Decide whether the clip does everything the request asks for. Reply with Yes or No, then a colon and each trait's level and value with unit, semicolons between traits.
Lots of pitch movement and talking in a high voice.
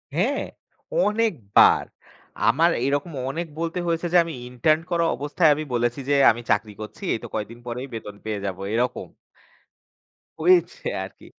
No: wide, 6.3 semitones; medium, 145 Hz